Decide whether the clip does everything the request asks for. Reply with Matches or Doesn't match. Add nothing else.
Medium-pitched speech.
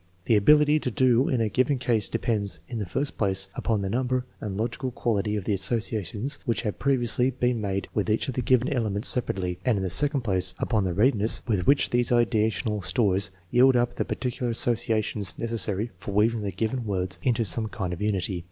Doesn't match